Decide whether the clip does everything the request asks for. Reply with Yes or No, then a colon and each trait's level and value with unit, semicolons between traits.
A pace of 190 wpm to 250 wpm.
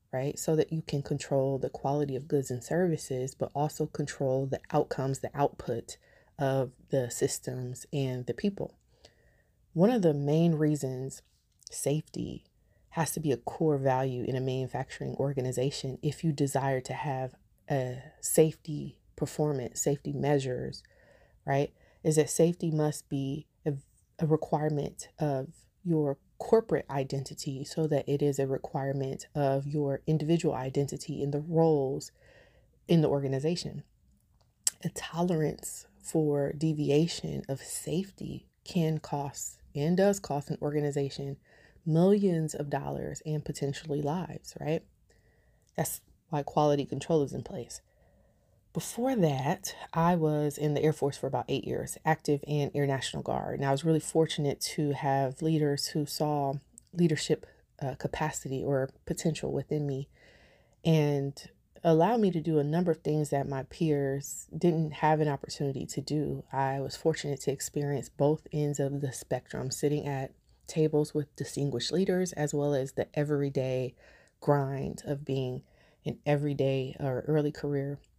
No: average, 145 wpm